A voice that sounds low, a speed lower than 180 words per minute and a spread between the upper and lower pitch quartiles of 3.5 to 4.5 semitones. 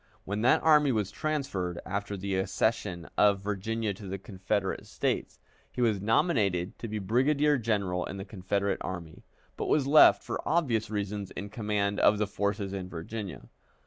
No: low, 105 Hz; average, 165 wpm; average, 2.8 semitones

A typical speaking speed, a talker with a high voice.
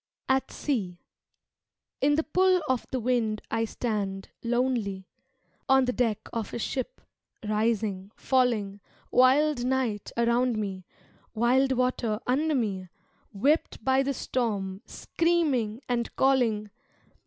No: slow, 120 wpm; high, 240 Hz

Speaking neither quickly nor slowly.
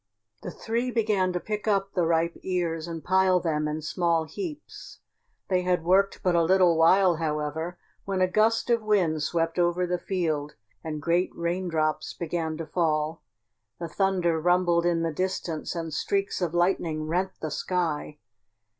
Yes: average, 165 wpm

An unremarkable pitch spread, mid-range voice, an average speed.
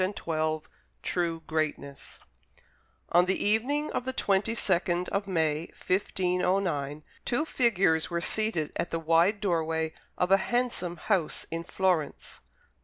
No: average, 3.6 semitones; medium, 180 Hz; slow, 125 wpm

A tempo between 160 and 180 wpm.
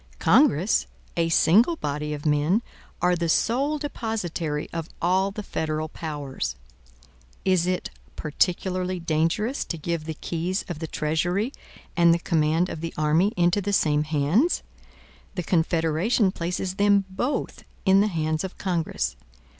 No: average, 140 wpm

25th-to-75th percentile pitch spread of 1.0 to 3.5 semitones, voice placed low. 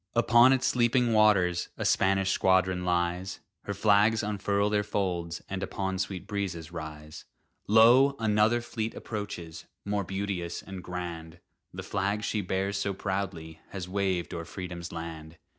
Yes: average, 3.0 semitones; very low, 95 Hz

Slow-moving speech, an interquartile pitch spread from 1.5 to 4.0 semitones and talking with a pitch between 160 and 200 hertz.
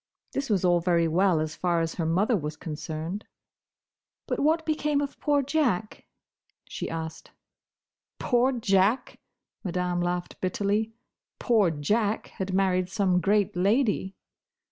No: slow, 130 wpm; average, 4.4 semitones; high, 190 Hz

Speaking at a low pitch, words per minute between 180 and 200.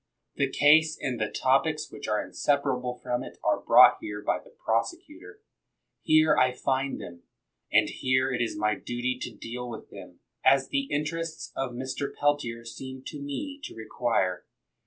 No: low, 130 Hz; average, 165 wpm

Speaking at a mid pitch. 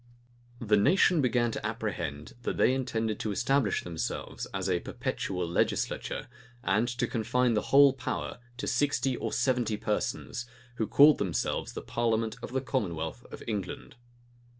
No: low, 115 Hz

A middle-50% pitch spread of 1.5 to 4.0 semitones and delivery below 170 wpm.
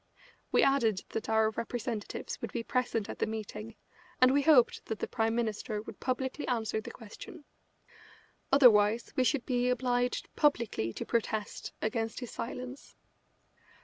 Yes: narrow, 2.6 semitones; average, 145 wpm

